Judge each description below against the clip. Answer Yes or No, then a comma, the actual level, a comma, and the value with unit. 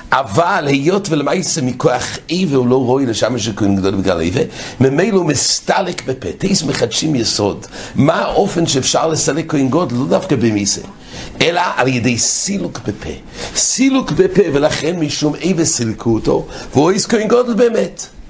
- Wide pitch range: Yes, wide, 6.1 semitones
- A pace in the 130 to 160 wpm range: Yes, average, 150 wpm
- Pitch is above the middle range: No, medium, 145 Hz